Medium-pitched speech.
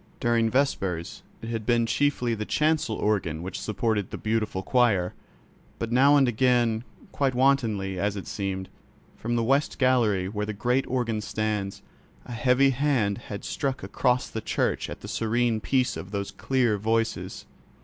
No: low, 115 Hz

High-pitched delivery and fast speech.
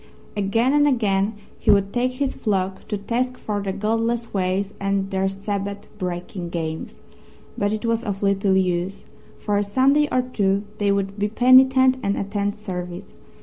No: high, 200 Hz; average, 165 wpm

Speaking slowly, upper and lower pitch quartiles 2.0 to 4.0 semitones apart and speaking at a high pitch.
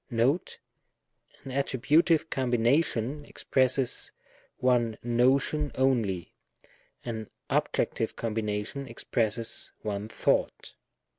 No: slow, 75 wpm; average, 3.3 semitones; low, 125 Hz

